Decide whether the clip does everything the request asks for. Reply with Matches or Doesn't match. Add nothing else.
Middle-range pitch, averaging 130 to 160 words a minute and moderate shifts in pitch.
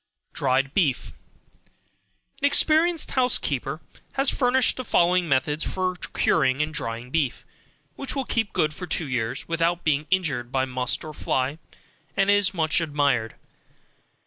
Doesn't match